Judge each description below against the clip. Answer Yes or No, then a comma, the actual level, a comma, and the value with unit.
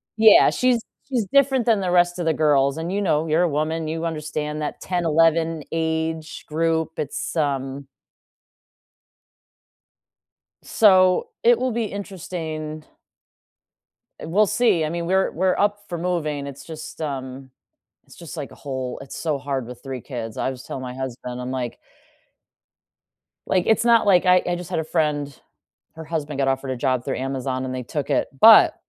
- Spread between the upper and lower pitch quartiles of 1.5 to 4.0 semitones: No, average, 4.6 semitones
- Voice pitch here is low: No, medium, 160 Hz